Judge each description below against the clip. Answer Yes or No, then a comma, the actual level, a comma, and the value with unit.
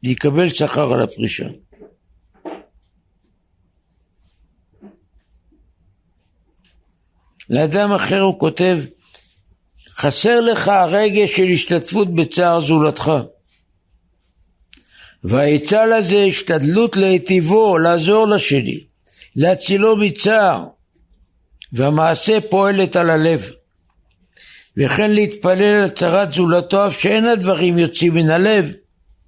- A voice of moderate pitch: Yes, medium, 165 Hz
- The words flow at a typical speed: No, slow, 80 wpm